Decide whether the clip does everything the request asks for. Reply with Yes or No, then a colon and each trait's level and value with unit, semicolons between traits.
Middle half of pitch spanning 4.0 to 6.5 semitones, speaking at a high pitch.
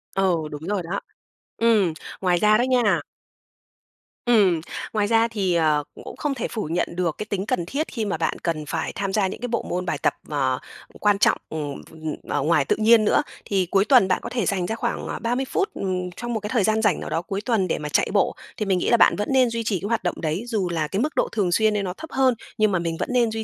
Yes: average, 4.7 semitones; high, 200 Hz